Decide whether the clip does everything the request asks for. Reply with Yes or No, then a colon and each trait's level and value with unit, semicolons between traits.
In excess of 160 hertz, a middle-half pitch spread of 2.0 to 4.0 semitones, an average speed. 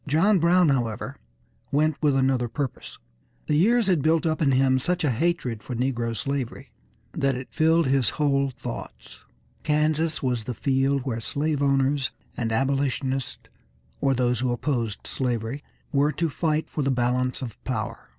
No: low, 135 Hz; average, 3.3 semitones; average, 160 wpm